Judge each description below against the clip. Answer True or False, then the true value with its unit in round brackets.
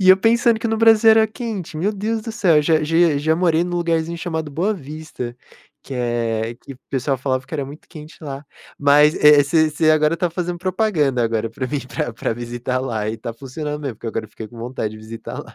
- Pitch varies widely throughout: True (5.7 semitones)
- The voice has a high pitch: False (150 Hz)